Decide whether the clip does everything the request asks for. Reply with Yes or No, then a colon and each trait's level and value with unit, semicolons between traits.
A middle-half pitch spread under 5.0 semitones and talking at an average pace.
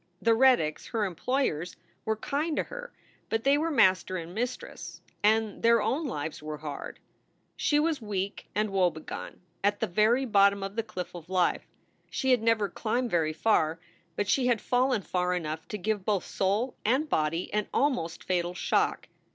No: wide, 5.5 semitones; average, 170 wpm